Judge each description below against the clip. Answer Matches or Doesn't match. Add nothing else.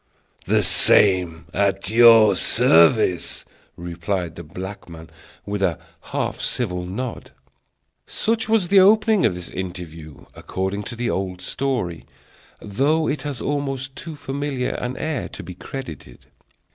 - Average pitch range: Doesn't match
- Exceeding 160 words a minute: Doesn't match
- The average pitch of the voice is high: Doesn't match